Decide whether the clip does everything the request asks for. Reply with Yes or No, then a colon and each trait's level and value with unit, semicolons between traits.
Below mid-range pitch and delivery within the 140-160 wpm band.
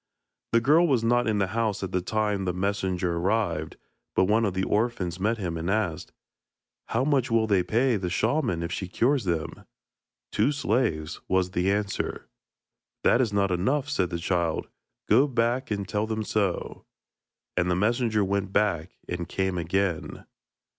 No: low, 100 Hz; average, 175 wpm